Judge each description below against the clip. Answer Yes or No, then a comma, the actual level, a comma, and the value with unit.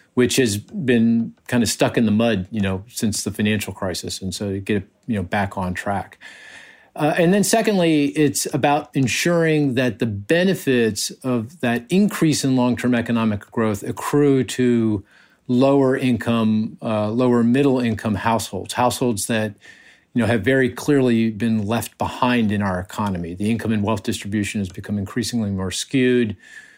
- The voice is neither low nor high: No, low, 115 Hz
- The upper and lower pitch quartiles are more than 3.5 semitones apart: Yes, average, 3.9 semitones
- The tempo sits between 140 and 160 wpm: Yes, average, 155 wpm